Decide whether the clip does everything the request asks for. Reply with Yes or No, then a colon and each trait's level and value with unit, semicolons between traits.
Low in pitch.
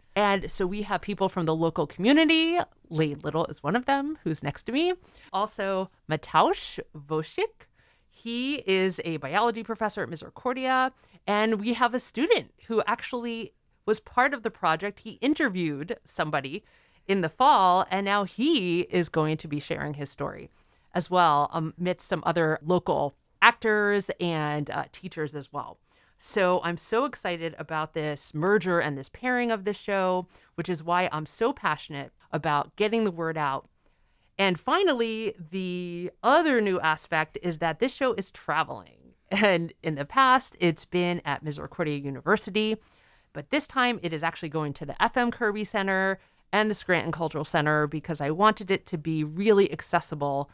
No: medium, 180 Hz